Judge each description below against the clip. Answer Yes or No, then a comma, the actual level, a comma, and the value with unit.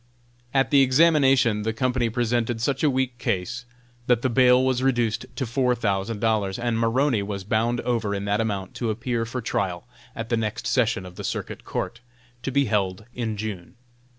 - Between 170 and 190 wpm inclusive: Yes, average, 185 wpm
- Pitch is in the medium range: No, low, 115 Hz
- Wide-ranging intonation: No, average, 2.9 semitones